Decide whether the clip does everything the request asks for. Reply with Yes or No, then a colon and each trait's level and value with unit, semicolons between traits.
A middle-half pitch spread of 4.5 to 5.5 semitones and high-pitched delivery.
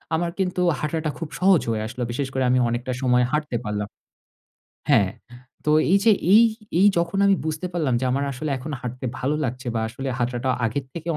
No: average, 4.8 semitones; low, 135 Hz